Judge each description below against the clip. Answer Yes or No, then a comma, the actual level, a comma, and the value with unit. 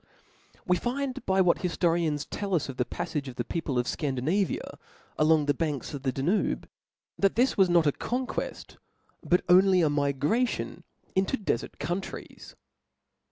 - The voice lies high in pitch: No, medium, 170 Hz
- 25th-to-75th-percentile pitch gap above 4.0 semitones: Yes, average, 5.1 semitones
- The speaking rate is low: No, average, 155 wpm